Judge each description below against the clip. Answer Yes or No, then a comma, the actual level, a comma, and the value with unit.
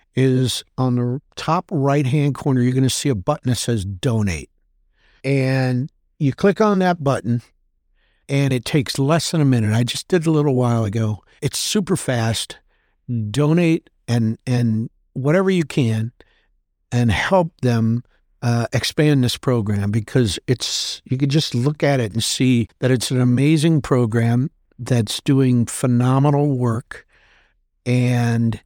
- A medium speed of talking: Yes, average, 155 wpm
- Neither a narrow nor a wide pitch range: Yes, average, 3.5 semitones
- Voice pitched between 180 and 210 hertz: No, low, 130 Hz